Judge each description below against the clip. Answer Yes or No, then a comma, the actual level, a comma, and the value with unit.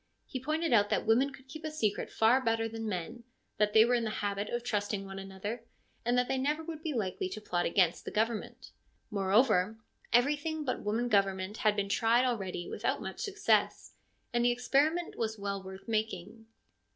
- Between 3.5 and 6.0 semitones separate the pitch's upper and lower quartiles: Yes, average, 3.8 semitones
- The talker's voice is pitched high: Yes, high, 225 Hz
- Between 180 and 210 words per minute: Yes, average, 190 wpm